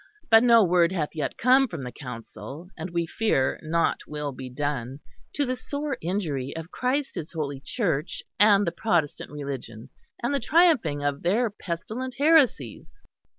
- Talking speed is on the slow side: No, average, 160 wpm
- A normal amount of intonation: No, wide, 8.5 semitones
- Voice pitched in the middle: Yes, medium, 170 Hz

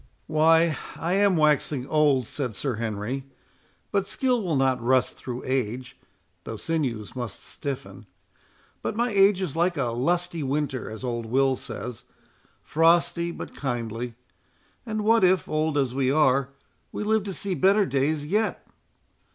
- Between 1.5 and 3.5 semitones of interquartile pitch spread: No, wide, 5.6 semitones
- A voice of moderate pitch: Yes, medium, 145 Hz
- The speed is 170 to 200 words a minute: No, average, 150 wpm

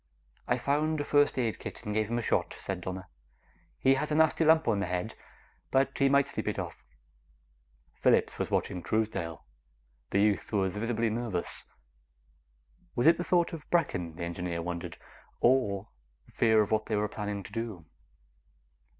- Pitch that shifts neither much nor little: No, wide, 6.1 semitones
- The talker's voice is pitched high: No, low, 110 Hz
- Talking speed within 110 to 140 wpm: No, average, 170 wpm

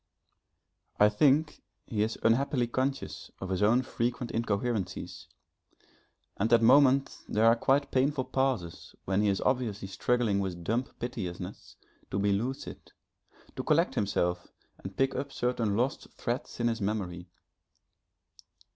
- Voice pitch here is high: No, low, 115 Hz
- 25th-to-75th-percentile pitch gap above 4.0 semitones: Yes, average, 4.6 semitones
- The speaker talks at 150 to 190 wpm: No, slow, 135 wpm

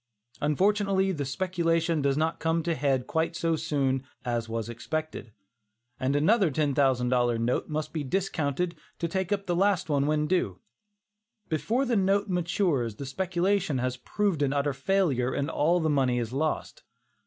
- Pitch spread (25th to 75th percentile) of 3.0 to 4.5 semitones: No, average, 5.1 semitones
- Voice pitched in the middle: Yes, medium, 155 Hz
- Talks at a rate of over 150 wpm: Yes, average, 165 wpm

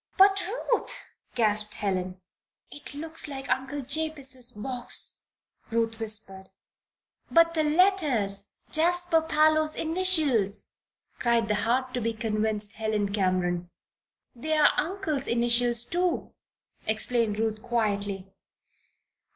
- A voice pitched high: Yes, high, 240 Hz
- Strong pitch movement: Yes, wide, 6.6 semitones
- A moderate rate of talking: No, slow, 100 wpm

